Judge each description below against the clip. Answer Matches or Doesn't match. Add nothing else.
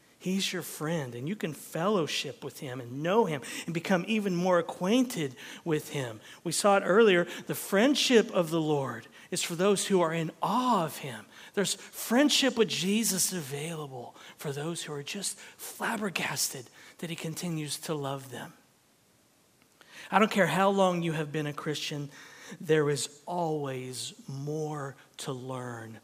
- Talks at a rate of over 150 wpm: Matches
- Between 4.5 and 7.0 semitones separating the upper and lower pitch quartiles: Matches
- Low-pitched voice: Doesn't match